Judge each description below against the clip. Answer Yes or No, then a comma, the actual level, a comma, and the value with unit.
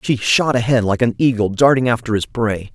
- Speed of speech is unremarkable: No, fast, 220 wpm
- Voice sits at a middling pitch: No, low, 115 Hz